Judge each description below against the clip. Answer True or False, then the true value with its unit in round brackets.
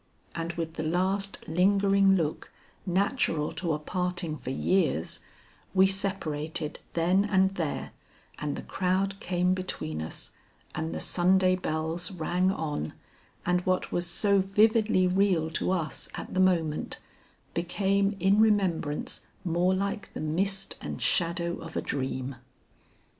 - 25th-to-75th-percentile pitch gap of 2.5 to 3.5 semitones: True (3.1 semitones)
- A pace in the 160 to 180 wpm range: False (135 wpm)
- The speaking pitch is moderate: True (180 Hz)